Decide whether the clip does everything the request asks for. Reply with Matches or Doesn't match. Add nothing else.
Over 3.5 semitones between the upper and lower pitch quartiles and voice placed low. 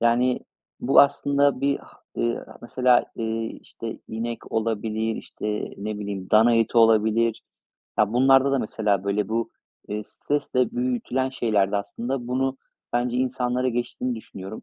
Doesn't match